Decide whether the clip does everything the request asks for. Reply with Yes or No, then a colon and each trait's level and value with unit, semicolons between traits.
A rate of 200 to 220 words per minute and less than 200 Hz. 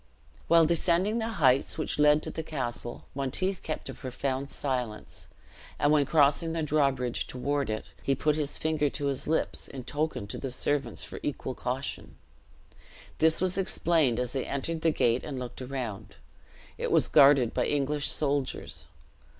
No: average, 165 wpm; medium, 140 Hz